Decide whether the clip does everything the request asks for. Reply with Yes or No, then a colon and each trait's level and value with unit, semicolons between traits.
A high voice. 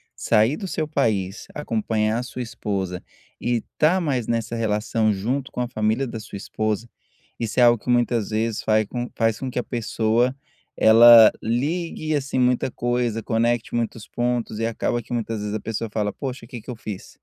No: low, 115 Hz